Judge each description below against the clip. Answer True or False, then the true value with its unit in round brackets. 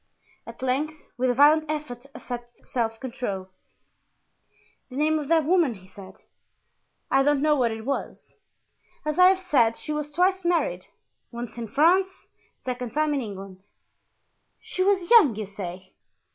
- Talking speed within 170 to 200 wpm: False (160 wpm)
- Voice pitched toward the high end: True (275 Hz)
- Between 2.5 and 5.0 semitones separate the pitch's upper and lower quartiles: False (5.4 semitones)